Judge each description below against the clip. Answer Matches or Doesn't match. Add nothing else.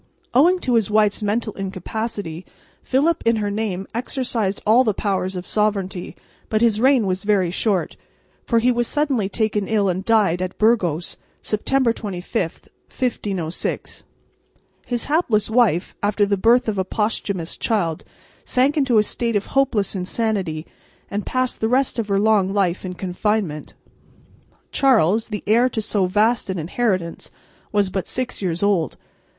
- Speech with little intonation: Doesn't match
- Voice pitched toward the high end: Matches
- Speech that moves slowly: Doesn't match